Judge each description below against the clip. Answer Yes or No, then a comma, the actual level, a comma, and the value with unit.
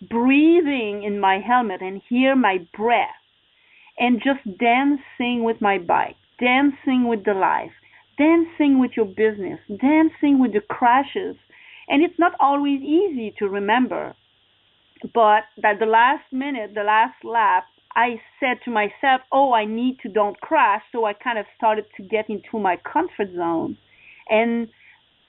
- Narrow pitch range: No, average, 4.6 semitones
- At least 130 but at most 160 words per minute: Yes, average, 150 wpm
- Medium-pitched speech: No, high, 240 Hz